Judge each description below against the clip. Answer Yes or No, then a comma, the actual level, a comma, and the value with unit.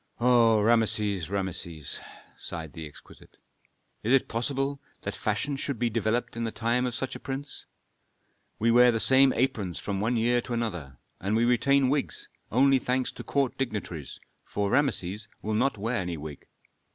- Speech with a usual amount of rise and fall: Yes, average, 4.3 semitones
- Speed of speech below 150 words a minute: No, average, 165 wpm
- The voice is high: No, low, 115 Hz